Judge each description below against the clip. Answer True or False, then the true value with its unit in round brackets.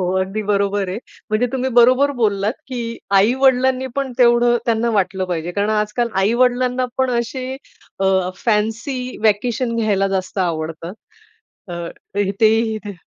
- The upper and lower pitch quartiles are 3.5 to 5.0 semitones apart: True (4.2 semitones)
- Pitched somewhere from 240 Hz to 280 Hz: False (220 Hz)